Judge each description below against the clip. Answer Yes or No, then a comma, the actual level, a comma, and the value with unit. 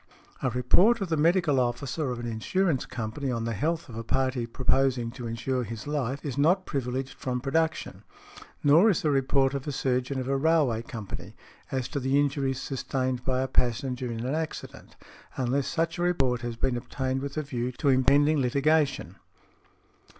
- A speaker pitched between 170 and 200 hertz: No, low, 135 Hz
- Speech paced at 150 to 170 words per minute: No, average, 180 wpm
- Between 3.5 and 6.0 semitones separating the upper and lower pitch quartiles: No, average, 2.9 semitones